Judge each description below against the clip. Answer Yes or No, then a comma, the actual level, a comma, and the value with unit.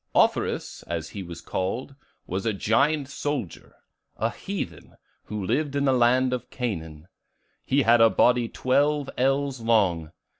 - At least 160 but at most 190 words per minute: No, average, 145 wpm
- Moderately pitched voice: No, low, 120 Hz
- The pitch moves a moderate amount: No, wide, 6.0 semitones